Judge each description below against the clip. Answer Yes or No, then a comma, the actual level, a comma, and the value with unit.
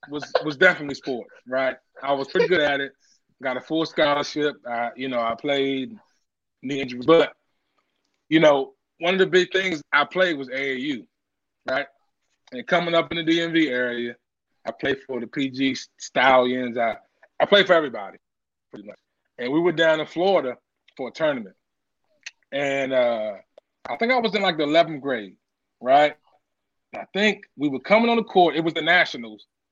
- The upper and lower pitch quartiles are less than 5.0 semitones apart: No, average, 5.3 semitones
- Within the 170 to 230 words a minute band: Yes, average, 180 wpm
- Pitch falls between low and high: Yes, medium, 150 Hz